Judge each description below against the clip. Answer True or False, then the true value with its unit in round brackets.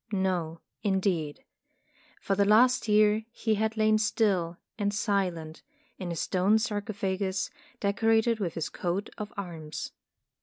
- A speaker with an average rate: False (125 wpm)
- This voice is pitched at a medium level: False (200 Hz)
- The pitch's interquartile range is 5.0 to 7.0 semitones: False (3.1 semitones)